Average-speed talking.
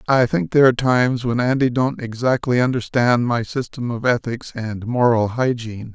Yes: average, 170 wpm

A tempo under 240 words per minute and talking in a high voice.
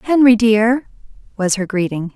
Yes: average, 140 wpm; high, 220 Hz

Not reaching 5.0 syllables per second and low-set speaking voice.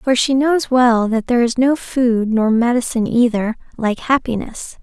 No: 4.6 syllables/s; high, 240 Hz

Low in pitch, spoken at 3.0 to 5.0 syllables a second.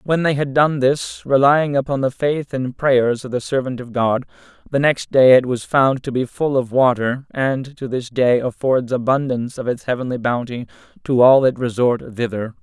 Yes: low, 130 Hz; 4.8 syllables/s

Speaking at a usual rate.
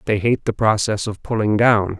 No: fast, 210 wpm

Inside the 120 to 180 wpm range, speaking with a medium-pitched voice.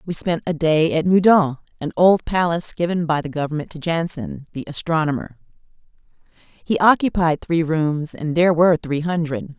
Yes: average, 165 wpm; medium, 165 Hz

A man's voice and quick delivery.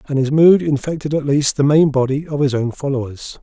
Yes: male; fast, 230 wpm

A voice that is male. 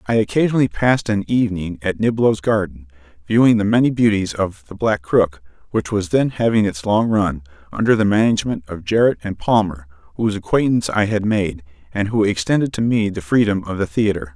Yes: male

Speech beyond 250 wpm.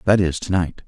Yes: fast, 275 wpm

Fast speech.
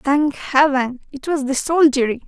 No: average, 160 wpm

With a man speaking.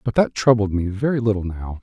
Yes: male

